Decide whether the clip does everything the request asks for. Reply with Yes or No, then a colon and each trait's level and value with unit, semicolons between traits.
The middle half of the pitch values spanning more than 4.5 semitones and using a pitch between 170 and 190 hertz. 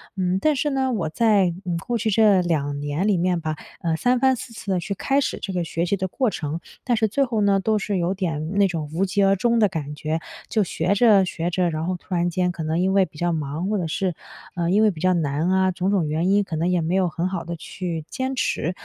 No: average, 3.6 semitones; medium, 185 Hz